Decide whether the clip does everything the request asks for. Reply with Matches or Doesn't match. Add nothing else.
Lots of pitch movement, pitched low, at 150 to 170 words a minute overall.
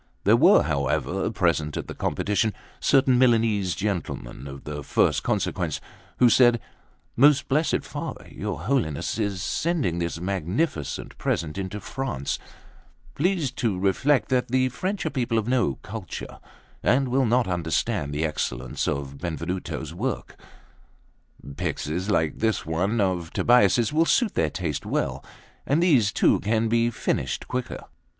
Doesn't match